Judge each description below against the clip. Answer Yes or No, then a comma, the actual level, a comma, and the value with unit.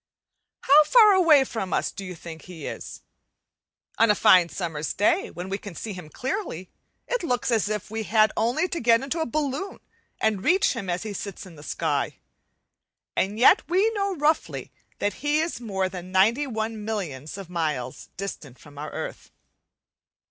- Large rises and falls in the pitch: Yes, wide, 7.7 semitones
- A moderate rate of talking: Yes, average, 180 wpm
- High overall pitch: Yes, high, 215 Hz